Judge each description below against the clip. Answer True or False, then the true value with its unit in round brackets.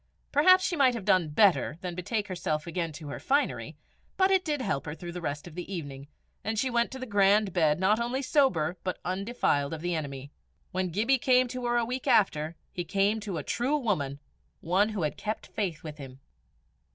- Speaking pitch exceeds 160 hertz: True (190 Hz)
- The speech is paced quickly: True (215 wpm)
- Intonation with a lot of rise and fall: True (6.9 semitones)